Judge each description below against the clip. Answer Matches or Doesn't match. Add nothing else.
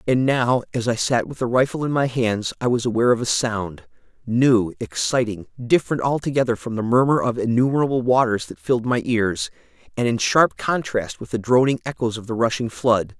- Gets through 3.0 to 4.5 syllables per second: Doesn't match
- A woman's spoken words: Doesn't match